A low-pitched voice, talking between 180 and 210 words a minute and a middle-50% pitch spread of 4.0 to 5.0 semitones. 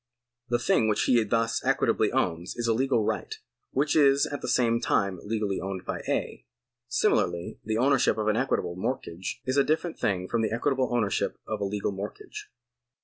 Yes: low, 115 Hz; average, 185 wpm; average, 4.6 semitones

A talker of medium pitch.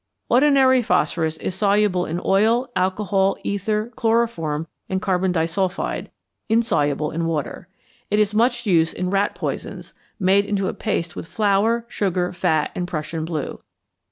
No: high, 195 Hz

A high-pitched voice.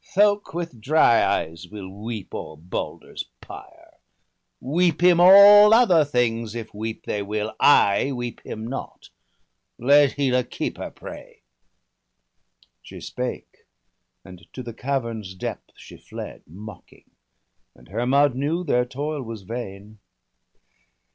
No: low, 120 Hz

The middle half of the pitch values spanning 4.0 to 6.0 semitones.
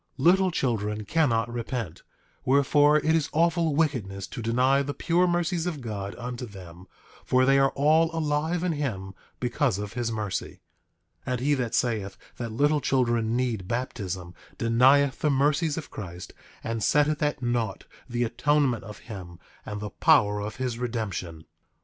Yes: wide, 5.5 semitones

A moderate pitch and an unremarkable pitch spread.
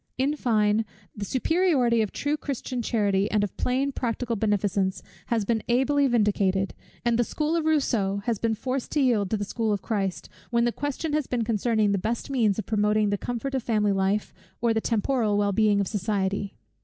No: high, 225 Hz; average, 3.6 semitones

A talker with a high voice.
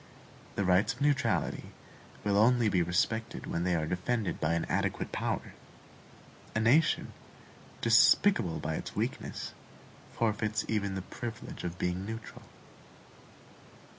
No: low, 105 Hz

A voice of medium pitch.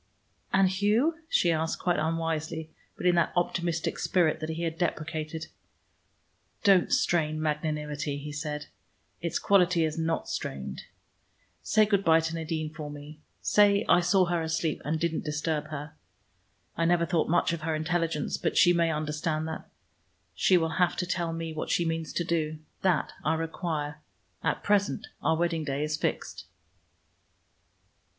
Yes: medium, 165 Hz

